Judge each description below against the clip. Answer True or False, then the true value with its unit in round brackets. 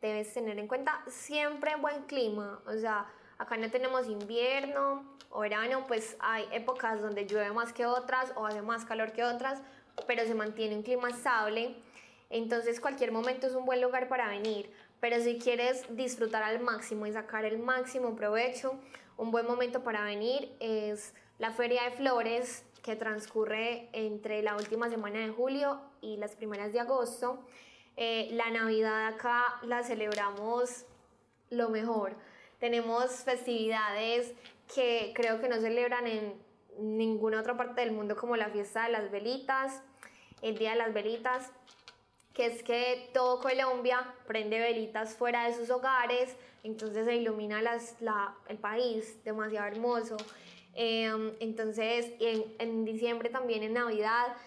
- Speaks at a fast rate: False (150 wpm)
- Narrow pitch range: True (2.2 semitones)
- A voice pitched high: True (235 Hz)